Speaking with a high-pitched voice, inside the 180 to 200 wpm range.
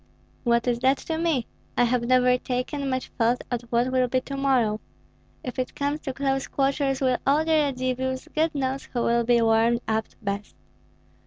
Yes: very high, 255 Hz; average, 185 wpm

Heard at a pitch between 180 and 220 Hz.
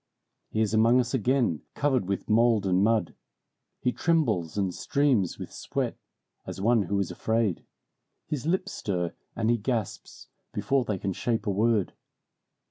No: low, 110 Hz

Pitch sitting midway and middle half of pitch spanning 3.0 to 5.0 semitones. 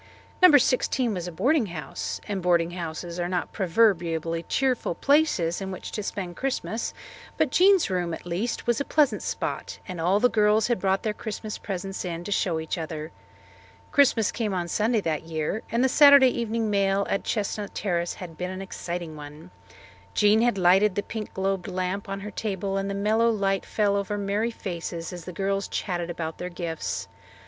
No: high, 195 Hz; average, 3.9 semitones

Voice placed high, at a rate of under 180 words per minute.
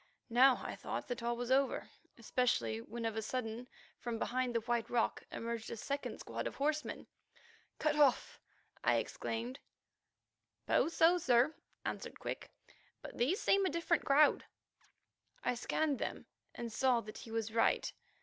Yes: high, 245 Hz; average, 155 wpm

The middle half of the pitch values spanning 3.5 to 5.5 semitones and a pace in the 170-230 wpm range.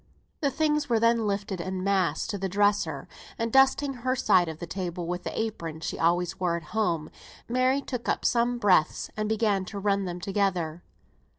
Yes: average, 4.7 semitones; average, 190 wpm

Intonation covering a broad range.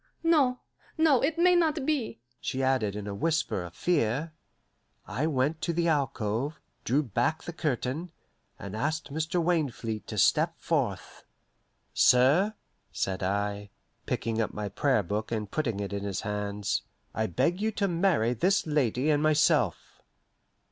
Yes: wide, 7.9 semitones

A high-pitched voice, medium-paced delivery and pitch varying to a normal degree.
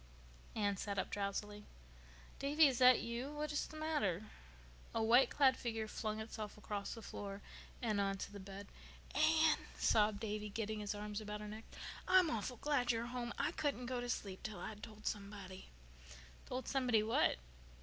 Yes: high, 220 Hz; average, 175 wpm; average, 3.4 semitones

